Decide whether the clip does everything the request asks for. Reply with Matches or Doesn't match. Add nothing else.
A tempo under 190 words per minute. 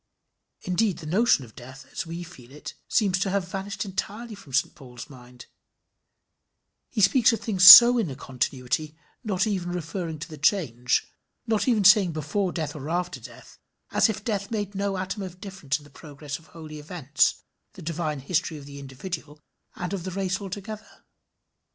Matches